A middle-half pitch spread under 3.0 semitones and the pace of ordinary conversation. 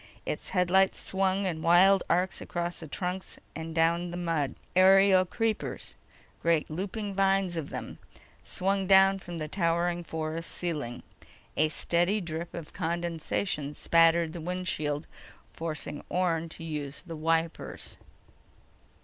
No: narrow, 2.5 semitones; slow, 125 wpm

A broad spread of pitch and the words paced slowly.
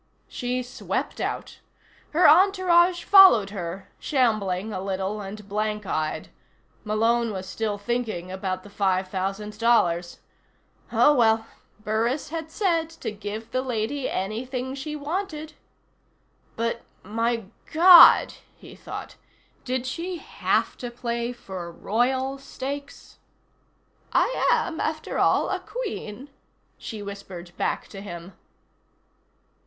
Yes: wide, 5.9 semitones; slow, 115 wpm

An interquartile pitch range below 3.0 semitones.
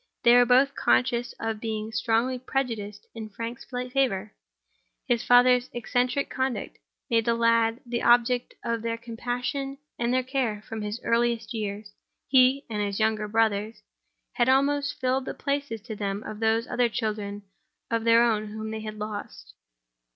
Yes: narrow, 2.5 semitones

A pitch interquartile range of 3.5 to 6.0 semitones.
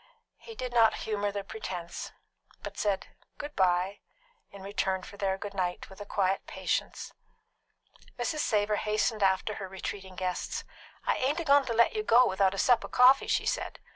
Yes: average, 4.0 semitones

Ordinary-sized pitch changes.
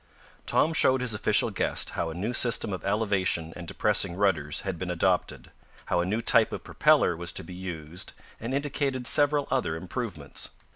No: wide, 5.9 semitones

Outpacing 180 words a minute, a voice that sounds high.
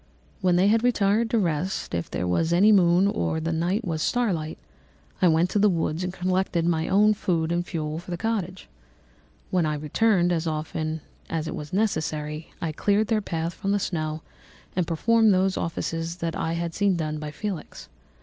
No: average, 195 wpm; medium, 175 Hz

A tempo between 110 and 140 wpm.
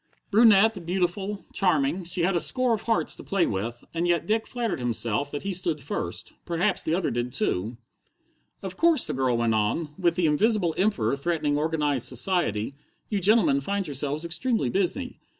No: average, 175 wpm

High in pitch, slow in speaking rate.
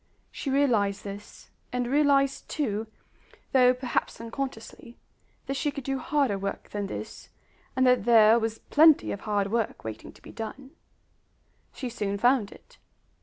No: high, 240 Hz; average, 150 wpm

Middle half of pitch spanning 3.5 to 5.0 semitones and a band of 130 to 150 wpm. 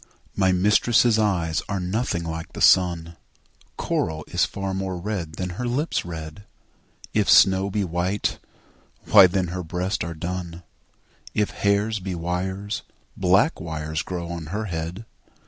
No: average, 3.0 semitones; average, 145 wpm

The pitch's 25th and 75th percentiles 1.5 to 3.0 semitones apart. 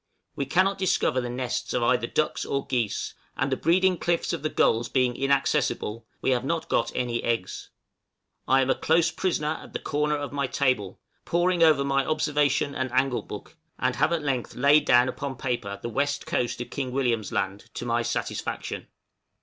No: average, 3.7 semitones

